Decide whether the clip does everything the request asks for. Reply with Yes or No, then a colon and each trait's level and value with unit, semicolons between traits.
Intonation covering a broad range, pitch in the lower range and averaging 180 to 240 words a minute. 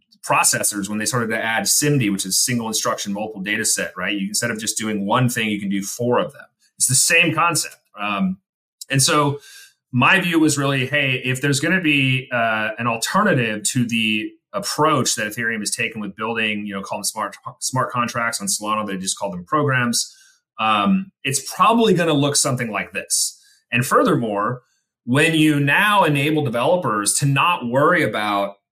Yes: wide, 5.8 semitones; low, 120 Hz; average, 190 wpm